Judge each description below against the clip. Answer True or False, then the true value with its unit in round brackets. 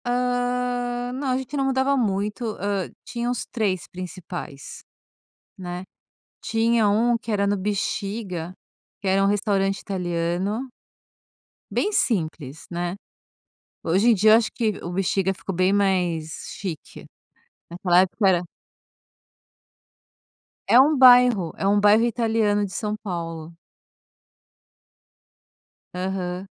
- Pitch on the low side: False (200 Hz)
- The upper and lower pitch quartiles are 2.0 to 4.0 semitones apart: False (4.5 semitones)